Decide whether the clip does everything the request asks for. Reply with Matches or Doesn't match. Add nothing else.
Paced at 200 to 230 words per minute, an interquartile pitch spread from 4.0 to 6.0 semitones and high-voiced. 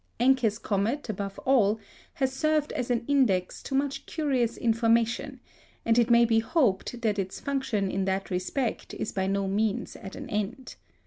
Doesn't match